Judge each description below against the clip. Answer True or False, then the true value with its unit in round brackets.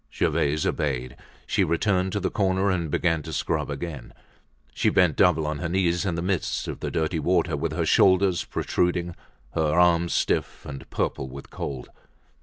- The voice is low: True (85 Hz)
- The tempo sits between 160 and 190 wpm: True (175 wpm)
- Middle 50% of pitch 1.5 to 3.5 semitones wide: True (3.2 semitones)